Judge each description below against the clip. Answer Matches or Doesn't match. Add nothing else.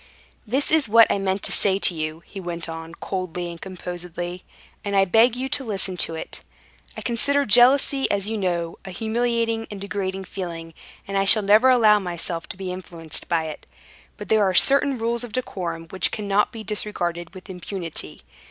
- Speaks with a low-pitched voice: Doesn't match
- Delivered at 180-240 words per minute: Matches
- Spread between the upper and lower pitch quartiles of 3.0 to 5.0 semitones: Matches